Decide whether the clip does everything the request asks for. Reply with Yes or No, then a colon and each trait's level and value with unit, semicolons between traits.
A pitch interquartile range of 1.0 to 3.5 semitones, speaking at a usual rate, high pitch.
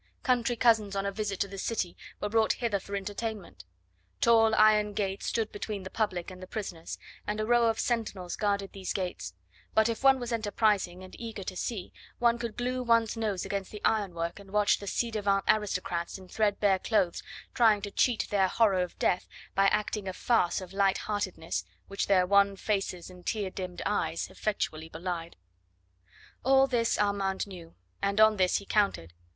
Yes: average, 2.8 semitones; average, 185 wpm; high, 200 Hz